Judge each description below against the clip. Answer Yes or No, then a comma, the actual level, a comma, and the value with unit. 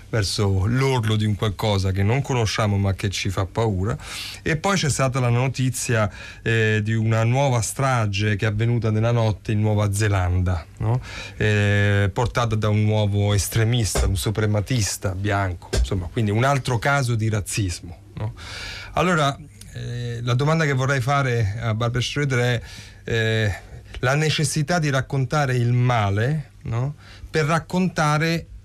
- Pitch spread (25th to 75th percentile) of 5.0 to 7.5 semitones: No, average, 4.1 semitones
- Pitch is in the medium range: No, low, 110 Hz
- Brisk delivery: No, average, 150 wpm